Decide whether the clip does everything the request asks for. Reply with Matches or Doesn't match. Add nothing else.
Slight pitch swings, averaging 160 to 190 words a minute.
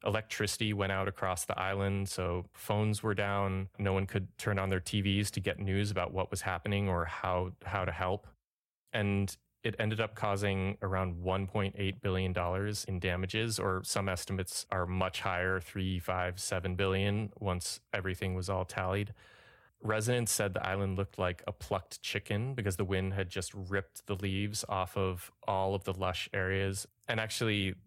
Matches